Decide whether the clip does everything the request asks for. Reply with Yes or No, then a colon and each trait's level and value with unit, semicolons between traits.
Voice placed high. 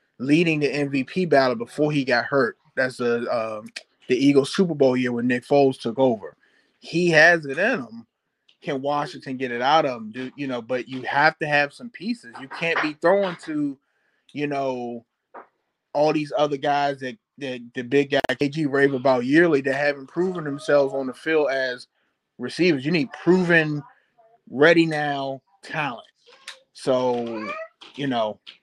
No: medium, 140 Hz